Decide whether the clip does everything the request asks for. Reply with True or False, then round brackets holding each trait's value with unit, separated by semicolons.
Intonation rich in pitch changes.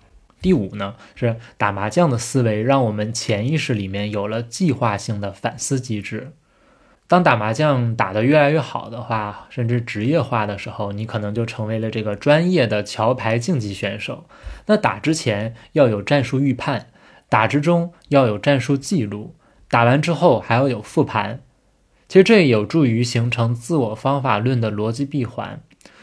False (4.9 semitones)